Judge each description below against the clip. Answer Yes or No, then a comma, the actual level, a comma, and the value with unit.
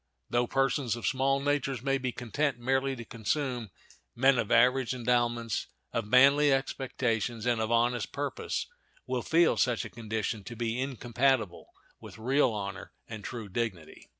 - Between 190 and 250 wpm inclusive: No, average, 150 wpm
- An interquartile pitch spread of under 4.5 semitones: Yes, average, 2.9 semitones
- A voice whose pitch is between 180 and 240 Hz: No, low, 120 Hz